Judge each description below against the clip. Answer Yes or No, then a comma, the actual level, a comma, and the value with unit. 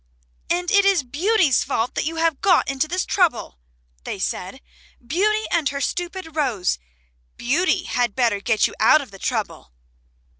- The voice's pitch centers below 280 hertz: No, very high, 310 Hz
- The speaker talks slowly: No, average, 160 wpm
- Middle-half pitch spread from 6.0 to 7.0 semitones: Yes, wide, 6.5 semitones